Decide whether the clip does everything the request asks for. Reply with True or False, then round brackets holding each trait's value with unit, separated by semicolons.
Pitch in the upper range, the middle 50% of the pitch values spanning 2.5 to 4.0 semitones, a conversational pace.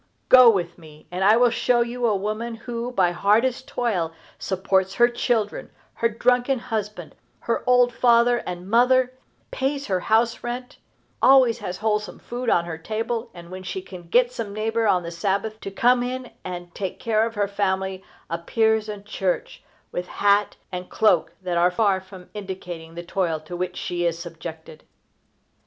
False (210 Hz; 4.7 semitones; 175 wpm)